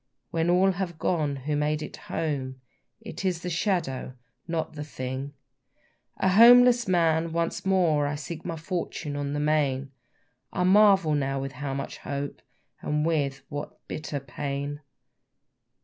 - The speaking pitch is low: No, medium, 155 Hz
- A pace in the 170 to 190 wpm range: No, average, 145 wpm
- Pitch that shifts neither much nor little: Yes, average, 3.7 semitones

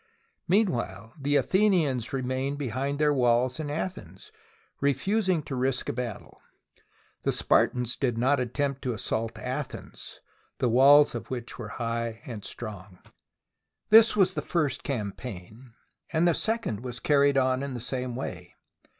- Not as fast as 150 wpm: Yes, average, 140 wpm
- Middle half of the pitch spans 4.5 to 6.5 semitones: No, average, 3.7 semitones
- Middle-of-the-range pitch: No, low, 130 Hz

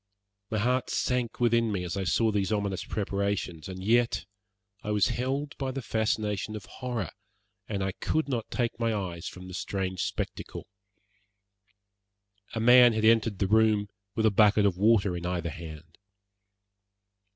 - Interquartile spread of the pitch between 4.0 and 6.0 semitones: No, average, 3.4 semitones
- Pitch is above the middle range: No, low, 105 Hz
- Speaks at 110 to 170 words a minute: Yes, average, 160 wpm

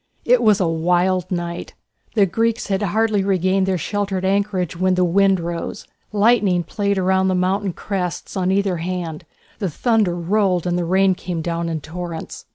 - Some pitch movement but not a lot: No, narrow, 2.3 semitones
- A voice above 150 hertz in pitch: Yes, medium, 185 Hz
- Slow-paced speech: No, average, 170 wpm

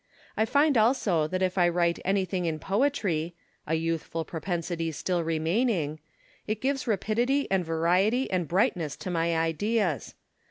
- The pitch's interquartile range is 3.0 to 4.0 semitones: No, average, 4.7 semitones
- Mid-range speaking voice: Yes, medium, 180 Hz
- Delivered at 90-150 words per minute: Yes, average, 145 wpm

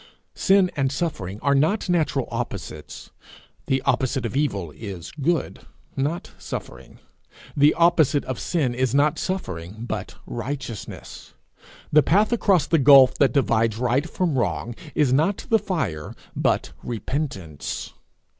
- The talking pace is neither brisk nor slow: No, slow, 130 wpm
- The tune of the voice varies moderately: No, wide, 5.7 semitones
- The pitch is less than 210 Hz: Yes, low, 135 Hz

